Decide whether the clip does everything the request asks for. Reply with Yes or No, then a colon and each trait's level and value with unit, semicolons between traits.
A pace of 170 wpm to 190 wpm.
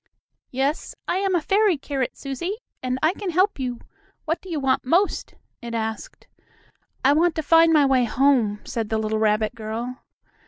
Yes: average, 180 wpm